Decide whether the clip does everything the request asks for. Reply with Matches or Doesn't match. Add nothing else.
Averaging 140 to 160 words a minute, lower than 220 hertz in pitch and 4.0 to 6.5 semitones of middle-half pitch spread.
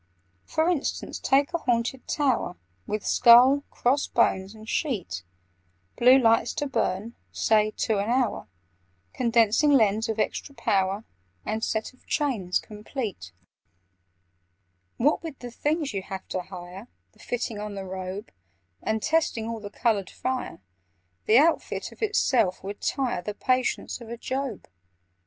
Doesn't match